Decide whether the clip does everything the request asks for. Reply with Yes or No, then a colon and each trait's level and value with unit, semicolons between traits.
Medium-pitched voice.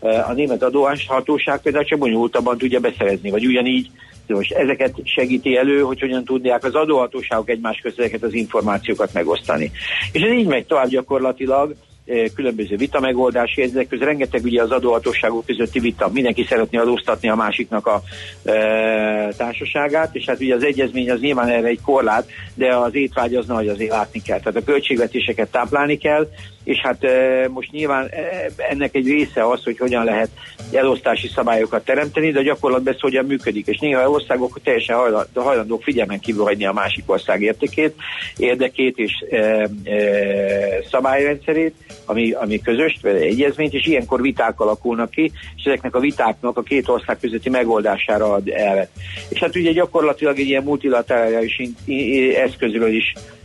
No: low, 125 Hz